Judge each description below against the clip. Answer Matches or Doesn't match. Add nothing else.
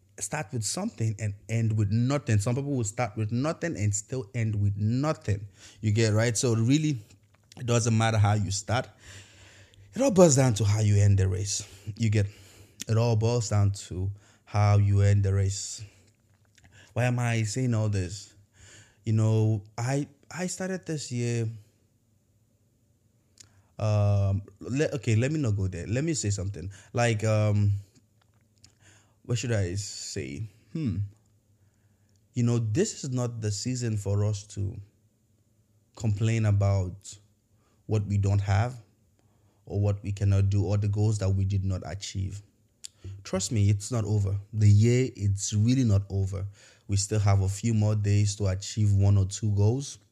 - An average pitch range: Doesn't match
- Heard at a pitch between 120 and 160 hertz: Doesn't match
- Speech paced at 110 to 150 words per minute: Doesn't match